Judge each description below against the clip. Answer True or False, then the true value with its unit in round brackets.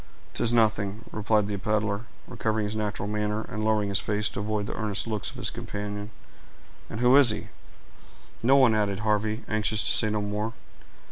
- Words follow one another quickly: False (185 wpm)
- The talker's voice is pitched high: False (105 Hz)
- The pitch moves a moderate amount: False (1.0 semitones)